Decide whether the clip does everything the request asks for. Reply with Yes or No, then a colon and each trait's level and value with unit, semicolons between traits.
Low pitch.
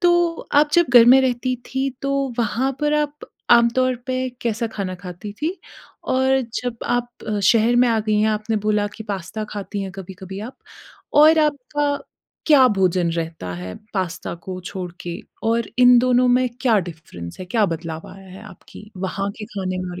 No: high, 220 Hz